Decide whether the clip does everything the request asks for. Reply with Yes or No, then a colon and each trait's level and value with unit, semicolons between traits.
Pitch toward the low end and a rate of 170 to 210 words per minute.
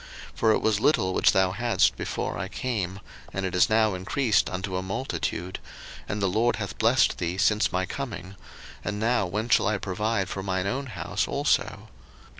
Yes: low, 100 Hz; average, 190 wpm